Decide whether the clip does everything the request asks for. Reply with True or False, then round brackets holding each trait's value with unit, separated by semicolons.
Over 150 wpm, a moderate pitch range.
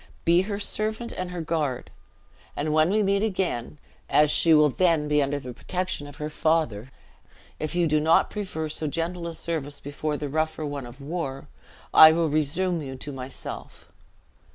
True (175 wpm; 3.2 semitones)